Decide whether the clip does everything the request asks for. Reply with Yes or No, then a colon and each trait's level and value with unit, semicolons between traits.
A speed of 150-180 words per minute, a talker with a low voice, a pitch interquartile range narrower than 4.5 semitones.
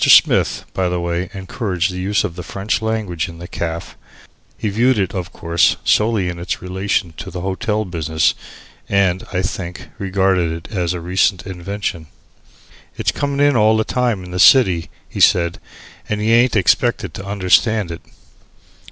Yes: average, 170 wpm; very low, 95 Hz; average, 3.3 semitones